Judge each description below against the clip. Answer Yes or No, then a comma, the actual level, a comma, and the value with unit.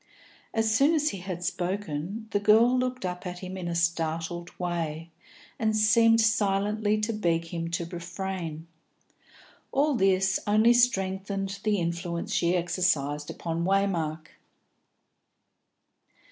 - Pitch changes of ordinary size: Yes, average, 4.0 semitones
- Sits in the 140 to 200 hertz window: Yes, high, 190 Hz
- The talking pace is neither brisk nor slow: No, slow, 125 wpm